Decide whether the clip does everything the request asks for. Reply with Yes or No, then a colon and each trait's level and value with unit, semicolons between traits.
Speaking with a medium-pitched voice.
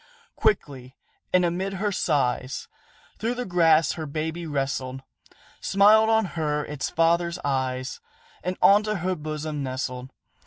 Yes: medium, 160 Hz